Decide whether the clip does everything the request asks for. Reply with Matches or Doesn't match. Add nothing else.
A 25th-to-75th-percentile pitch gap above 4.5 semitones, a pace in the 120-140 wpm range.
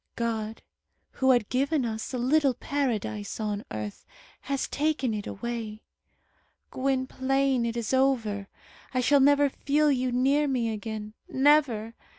Doesn't match